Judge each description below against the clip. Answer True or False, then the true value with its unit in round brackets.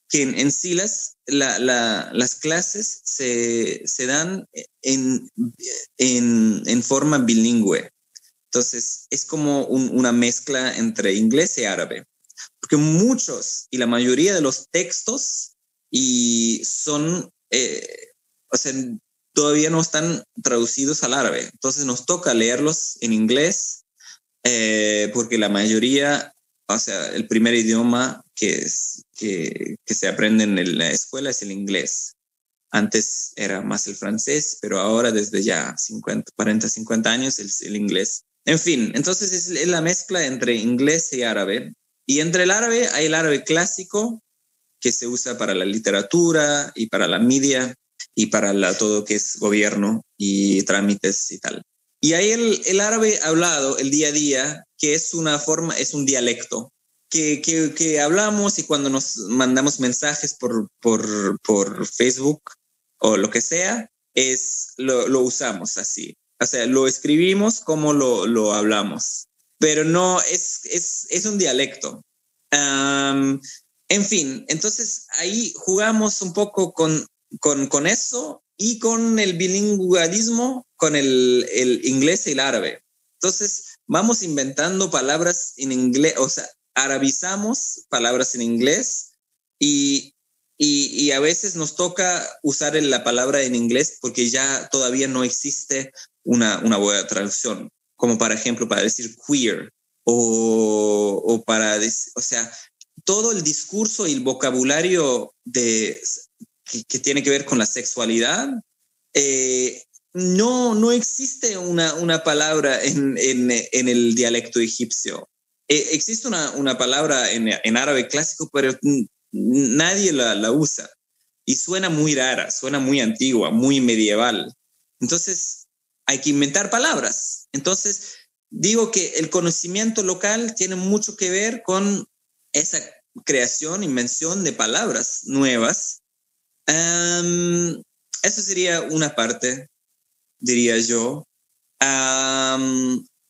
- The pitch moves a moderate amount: False (7.0 semitones)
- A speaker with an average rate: True (140 wpm)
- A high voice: False (145 Hz)